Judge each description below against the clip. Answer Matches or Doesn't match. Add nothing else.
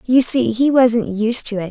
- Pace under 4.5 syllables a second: Matches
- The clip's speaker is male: Doesn't match